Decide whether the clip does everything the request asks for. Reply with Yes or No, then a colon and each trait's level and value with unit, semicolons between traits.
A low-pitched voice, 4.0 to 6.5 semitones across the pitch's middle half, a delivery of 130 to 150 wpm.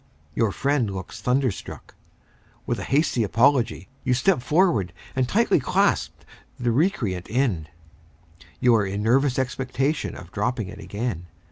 Yes: low, 120 Hz; average, 4.7 semitones; slow, 135 wpm